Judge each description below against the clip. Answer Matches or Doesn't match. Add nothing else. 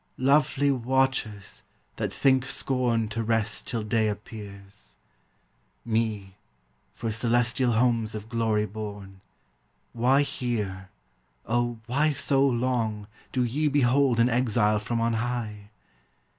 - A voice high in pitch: Doesn't match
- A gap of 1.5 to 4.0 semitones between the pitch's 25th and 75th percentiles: Matches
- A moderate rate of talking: Doesn't match